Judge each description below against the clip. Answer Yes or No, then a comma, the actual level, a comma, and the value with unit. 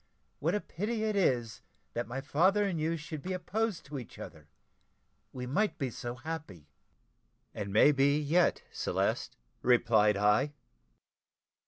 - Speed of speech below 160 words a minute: Yes, average, 145 wpm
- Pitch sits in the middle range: Yes, medium, 145 Hz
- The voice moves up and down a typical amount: No, wide, 6.9 semitones